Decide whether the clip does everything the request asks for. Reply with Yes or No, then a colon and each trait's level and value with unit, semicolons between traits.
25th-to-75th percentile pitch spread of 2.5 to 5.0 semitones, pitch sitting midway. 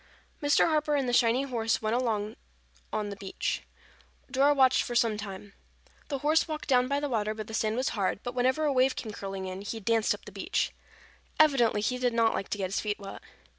No: average, 4.1 semitones; high, 230 Hz